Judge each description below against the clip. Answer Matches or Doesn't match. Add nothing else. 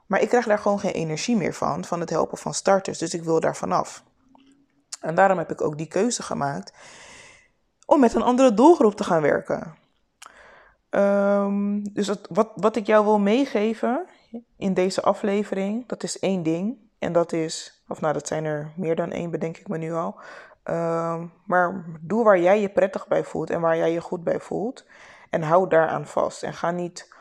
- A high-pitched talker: Matches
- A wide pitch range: Doesn't match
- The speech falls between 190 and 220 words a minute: Matches